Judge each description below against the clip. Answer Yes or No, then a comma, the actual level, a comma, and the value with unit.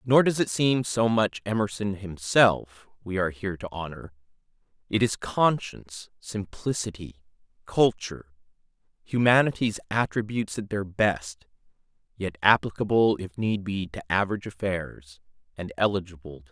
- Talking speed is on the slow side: Yes, slow, 125 wpm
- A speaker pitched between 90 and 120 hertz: Yes, low, 100 Hz